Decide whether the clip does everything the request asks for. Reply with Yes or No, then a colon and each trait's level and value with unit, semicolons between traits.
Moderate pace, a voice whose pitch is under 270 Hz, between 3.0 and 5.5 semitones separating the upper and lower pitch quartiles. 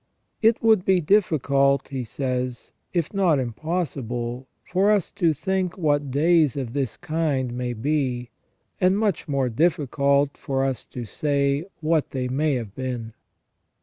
Yes: average, 150 wpm; medium, 140 Hz; average, 4.7 semitones